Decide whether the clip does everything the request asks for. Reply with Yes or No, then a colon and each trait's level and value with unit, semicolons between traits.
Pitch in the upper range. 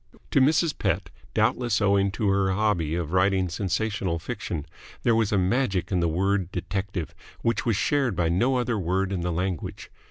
No: very low, 95 Hz